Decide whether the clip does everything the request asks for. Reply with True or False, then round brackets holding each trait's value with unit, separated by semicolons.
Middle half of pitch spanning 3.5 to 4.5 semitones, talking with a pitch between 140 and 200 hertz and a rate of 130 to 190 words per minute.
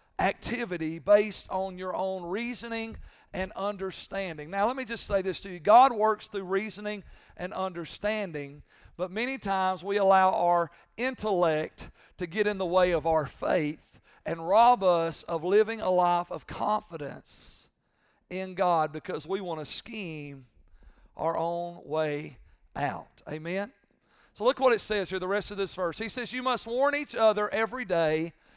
True (4.2 semitones; 190 Hz; 165 wpm)